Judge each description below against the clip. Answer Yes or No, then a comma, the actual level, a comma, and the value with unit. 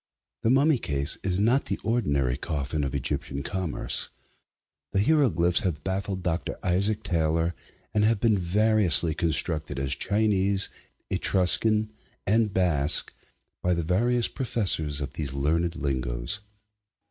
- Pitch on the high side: No, very low, 90 Hz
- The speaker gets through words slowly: Yes, slow, 125 wpm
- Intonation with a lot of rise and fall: Yes, wide, 5.9 semitones